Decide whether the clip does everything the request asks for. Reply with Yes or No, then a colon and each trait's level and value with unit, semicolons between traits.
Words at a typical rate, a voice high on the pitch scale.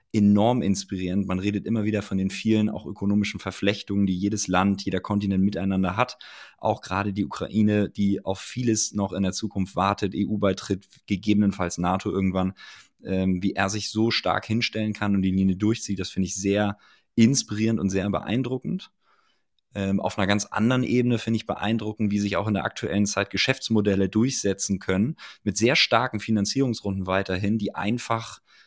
No: average, 170 wpm; low, 100 Hz